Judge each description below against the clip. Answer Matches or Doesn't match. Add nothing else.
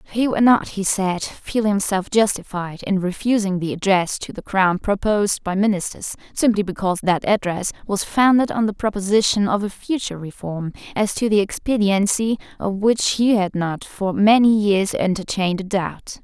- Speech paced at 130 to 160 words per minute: Doesn't match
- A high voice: Matches